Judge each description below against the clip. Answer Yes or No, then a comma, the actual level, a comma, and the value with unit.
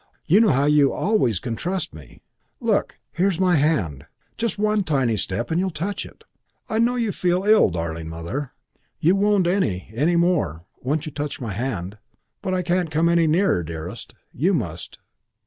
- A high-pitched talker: No, medium, 155 Hz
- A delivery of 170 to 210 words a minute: Yes, average, 180 wpm